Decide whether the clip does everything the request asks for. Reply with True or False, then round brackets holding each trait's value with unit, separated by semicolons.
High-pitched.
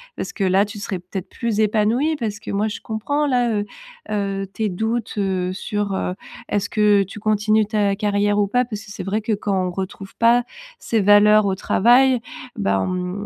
True (205 Hz)